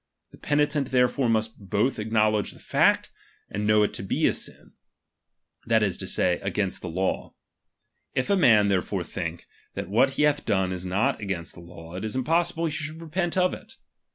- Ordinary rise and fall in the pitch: No, wide, 6.5 semitones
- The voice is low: Yes, low, 110 Hz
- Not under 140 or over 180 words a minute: No, average, 195 wpm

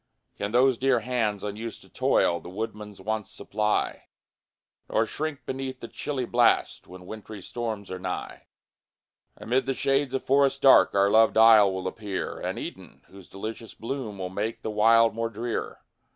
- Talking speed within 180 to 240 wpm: No, average, 165 wpm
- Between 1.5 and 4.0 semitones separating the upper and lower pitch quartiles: Yes, average, 3.4 semitones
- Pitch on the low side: Yes, low, 110 Hz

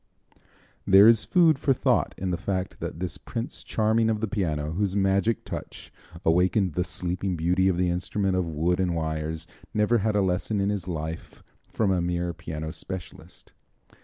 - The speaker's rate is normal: Yes, average, 175 wpm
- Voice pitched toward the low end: Yes, very low, 95 Hz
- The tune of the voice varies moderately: Yes, average, 3.1 semitones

